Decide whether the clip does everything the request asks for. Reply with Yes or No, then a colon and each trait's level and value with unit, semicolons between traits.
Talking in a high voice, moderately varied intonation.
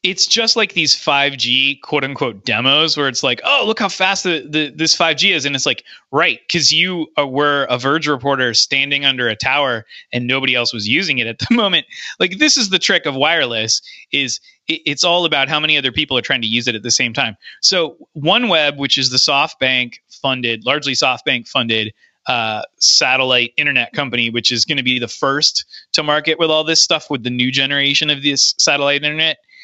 No: medium, 140 Hz; average, 4.2 semitones